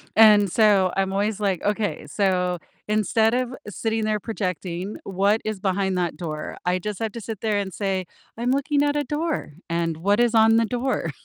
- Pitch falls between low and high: No, high, 205 Hz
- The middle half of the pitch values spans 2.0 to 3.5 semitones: Yes, average, 3.1 semitones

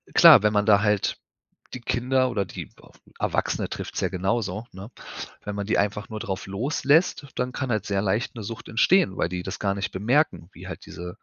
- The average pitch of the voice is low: Yes, low, 105 Hz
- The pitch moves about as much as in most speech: Yes, average, 3.9 semitones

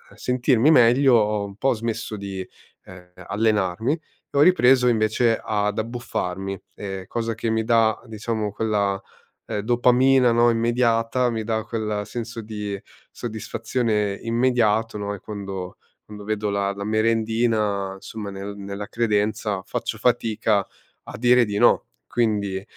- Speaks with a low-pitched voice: Yes, low, 110 Hz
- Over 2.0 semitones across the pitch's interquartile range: Yes, narrow, 2.5 semitones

